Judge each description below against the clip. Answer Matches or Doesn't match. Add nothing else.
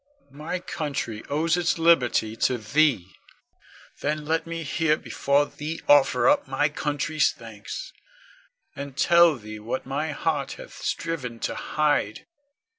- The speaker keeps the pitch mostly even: Doesn't match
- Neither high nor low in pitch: Matches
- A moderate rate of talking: Doesn't match